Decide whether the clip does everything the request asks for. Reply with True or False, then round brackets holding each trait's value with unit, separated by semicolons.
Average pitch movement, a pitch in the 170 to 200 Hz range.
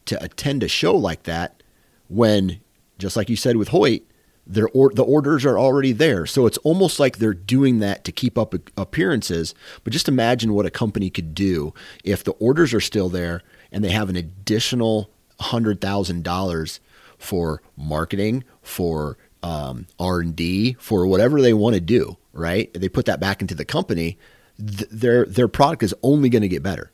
False (5.0 semitones; 105 Hz)